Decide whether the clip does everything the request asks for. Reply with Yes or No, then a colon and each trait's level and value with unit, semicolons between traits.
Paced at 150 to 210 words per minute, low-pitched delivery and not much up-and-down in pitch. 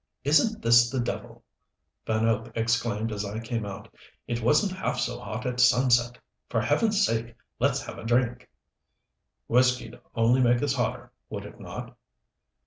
Yes: average, 155 wpm; low, 120 Hz; narrow, 1.9 semitones